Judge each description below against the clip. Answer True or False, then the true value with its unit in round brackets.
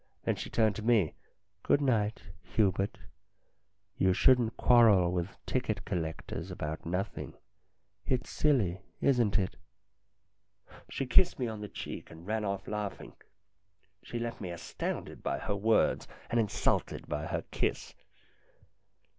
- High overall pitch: False (105 Hz)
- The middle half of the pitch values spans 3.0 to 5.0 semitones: True (4.2 semitones)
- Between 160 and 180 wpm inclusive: False (135 wpm)